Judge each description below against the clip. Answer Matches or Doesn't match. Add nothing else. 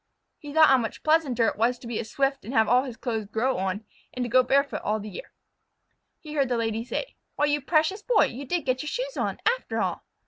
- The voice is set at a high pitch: Matches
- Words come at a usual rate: Doesn't match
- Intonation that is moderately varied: Matches